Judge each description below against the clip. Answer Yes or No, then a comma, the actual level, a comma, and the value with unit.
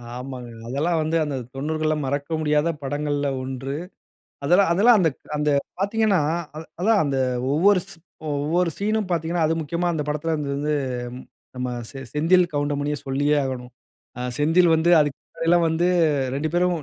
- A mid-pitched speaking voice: Yes, medium, 155 Hz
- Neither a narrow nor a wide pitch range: Yes, average, 3.3 semitones